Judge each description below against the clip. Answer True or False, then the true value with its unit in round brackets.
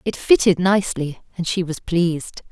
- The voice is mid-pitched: True (175 Hz)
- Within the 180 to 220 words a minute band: False (165 wpm)